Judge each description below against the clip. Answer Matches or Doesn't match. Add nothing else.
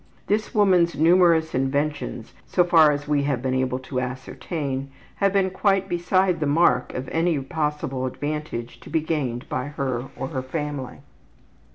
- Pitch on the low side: Doesn't match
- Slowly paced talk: Doesn't match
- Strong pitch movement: Doesn't match